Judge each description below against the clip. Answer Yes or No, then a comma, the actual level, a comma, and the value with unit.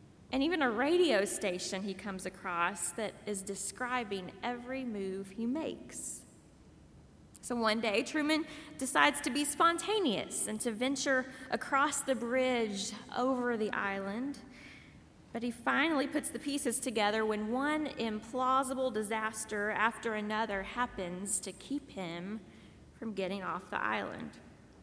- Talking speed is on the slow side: Yes, slow, 130 wpm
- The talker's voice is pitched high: Yes, high, 235 Hz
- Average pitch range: Yes, average, 4.5 semitones